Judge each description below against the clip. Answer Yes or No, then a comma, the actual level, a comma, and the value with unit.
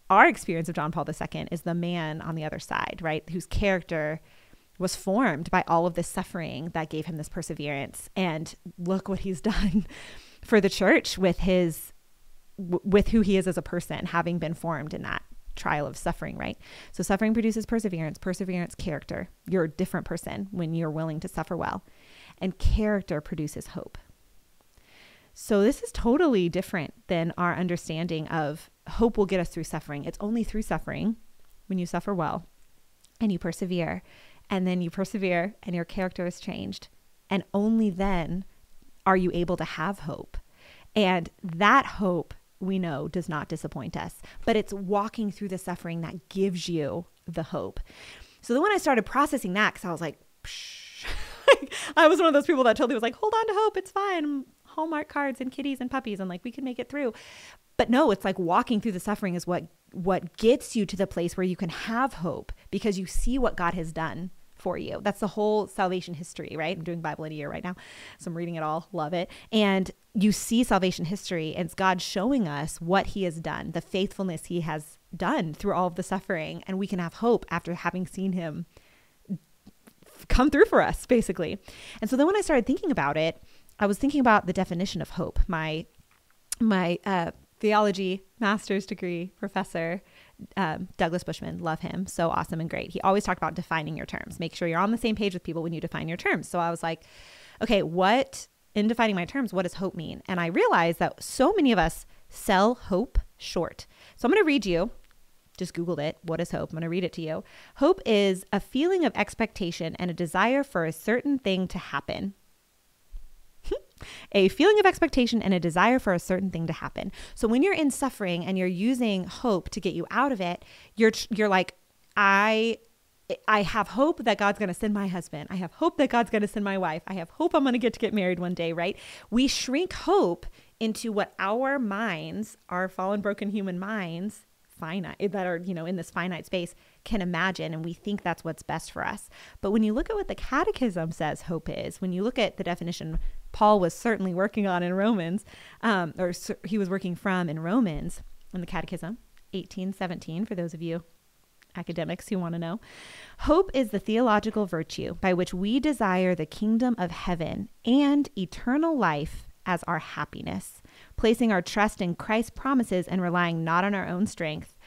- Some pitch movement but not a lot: Yes, average, 4.0 semitones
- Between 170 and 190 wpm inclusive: No, average, 200 wpm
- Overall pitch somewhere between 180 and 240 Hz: Yes, high, 190 Hz